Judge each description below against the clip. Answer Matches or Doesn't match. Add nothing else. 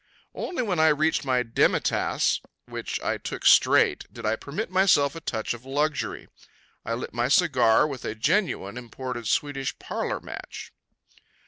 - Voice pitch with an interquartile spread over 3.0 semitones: Matches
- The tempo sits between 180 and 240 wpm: Doesn't match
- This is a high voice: Doesn't match